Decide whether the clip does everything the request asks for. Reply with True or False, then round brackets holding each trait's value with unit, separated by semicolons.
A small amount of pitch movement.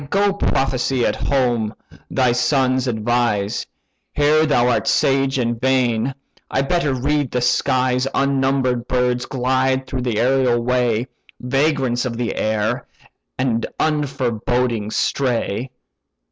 True (2.0 semitones)